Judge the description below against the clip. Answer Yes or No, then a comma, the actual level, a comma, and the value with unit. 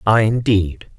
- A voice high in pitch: No, low, 105 Hz